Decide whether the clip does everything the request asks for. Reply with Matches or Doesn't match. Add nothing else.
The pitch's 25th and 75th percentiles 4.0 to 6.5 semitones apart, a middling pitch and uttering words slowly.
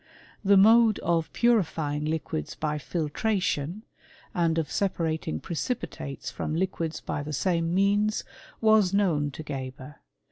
Matches